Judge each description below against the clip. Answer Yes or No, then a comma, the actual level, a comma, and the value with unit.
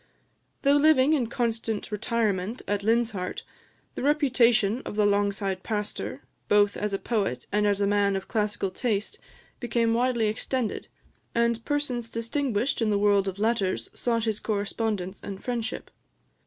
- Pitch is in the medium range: No, high, 220 Hz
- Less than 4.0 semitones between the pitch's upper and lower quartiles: Yes, average, 2.8 semitones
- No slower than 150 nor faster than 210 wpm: No, average, 140 wpm